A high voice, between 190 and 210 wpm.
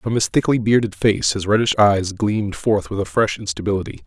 No: low, 100 Hz; fast, 205 wpm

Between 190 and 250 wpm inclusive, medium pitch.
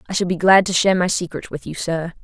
No: fast, 295 wpm; medium, 175 Hz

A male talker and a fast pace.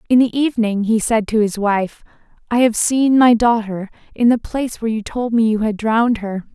No: female; fast, 220 wpm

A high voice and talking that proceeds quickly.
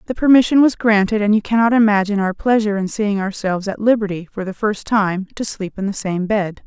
Yes: high, 205 Hz; fast, 225 wpm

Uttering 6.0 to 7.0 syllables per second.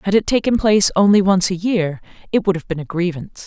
Yes: 6.3 syllables/s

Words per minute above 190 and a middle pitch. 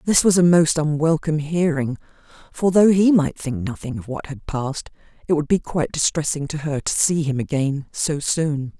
Yes: average, 200 wpm; medium, 155 Hz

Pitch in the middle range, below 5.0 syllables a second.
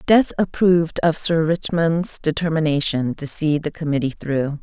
Yes: medium, 160 Hz; 4.6 syllables/s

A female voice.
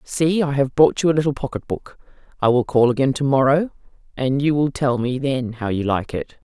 Yes: female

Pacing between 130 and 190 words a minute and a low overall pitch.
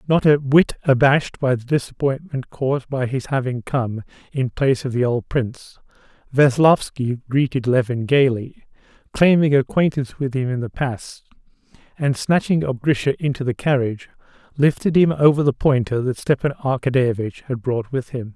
Yes: average, 155 wpm; low, 130 Hz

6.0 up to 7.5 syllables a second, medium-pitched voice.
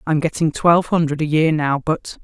No: 5.4 syllables/s; medium, 155 Hz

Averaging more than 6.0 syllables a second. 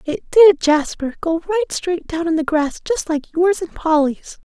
No: 4.7 syllables/s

